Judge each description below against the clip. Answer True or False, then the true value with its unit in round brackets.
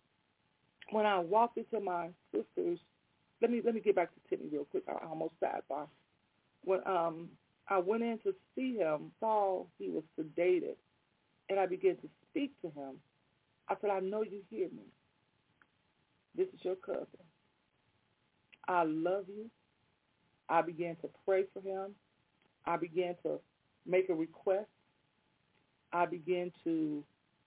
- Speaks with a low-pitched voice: False (190 Hz)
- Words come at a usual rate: True (150 wpm)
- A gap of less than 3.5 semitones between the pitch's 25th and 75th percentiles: False (4.2 semitones)